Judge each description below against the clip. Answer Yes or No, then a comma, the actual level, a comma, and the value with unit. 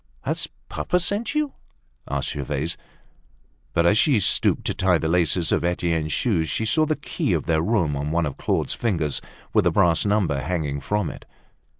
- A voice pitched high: No, very low, 85 Hz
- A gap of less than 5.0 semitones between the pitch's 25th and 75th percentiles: No, wide, 5.5 semitones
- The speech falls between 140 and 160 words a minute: No, average, 185 wpm